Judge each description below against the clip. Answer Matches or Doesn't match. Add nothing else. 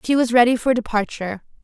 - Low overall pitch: Doesn't match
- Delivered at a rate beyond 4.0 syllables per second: Matches